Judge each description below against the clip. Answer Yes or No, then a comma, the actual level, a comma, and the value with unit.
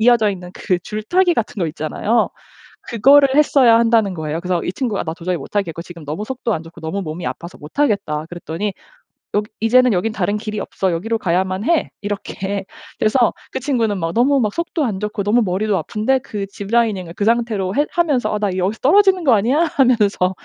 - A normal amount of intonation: Yes, average, 4.7 semitones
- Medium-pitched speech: No, high, 210 Hz